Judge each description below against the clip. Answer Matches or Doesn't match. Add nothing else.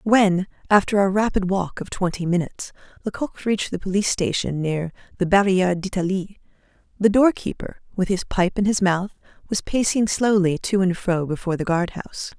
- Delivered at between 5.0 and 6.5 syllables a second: Matches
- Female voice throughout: Matches